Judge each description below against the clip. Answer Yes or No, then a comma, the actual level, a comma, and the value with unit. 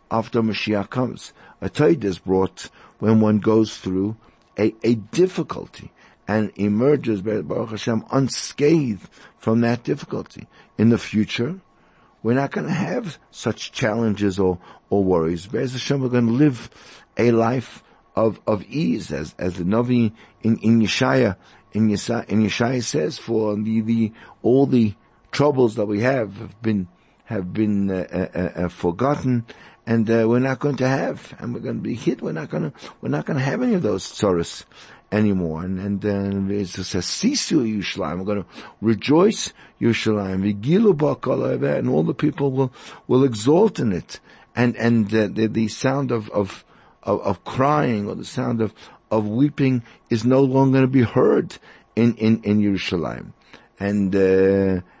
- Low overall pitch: Yes, low, 110 Hz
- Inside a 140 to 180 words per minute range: Yes, average, 165 wpm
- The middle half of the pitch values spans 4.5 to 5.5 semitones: No, average, 3.9 semitones